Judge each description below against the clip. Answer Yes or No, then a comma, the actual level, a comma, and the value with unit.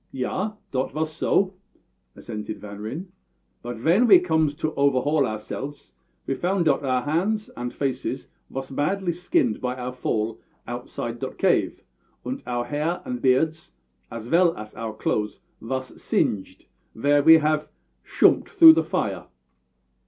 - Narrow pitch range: No, average, 5.0 semitones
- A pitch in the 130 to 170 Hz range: Yes, low, 135 Hz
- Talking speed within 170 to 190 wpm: No, average, 145 wpm